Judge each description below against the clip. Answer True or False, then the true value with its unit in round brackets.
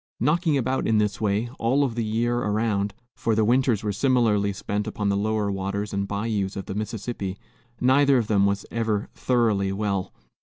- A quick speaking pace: False (185 wpm)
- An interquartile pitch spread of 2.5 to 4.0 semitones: True (2.9 semitones)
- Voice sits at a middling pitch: False (105 Hz)